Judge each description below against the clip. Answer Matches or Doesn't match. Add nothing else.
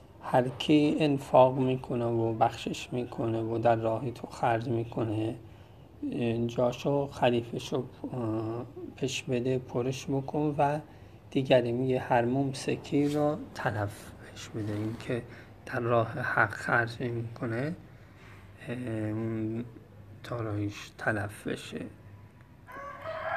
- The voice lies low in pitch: Matches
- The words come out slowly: Matches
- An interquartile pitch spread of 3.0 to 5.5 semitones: Doesn't match